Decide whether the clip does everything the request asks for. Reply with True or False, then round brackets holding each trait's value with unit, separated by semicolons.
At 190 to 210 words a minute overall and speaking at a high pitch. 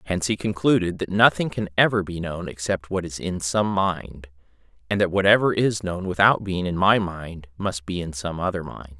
False (205 wpm; 90 Hz)